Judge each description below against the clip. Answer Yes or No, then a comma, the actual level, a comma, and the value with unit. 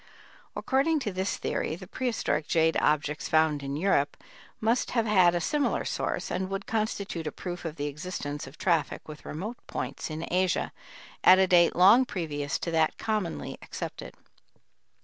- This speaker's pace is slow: No, average, 165 wpm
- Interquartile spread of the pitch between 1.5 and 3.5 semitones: No, average, 4.7 semitones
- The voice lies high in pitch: No, medium, 175 Hz